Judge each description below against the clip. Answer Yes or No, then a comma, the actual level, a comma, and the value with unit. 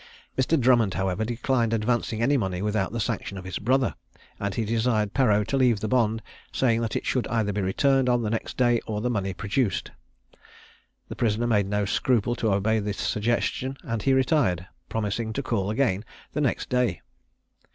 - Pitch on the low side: Yes, low, 115 Hz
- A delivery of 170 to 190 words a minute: Yes, average, 185 wpm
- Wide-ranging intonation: No, average, 3.2 semitones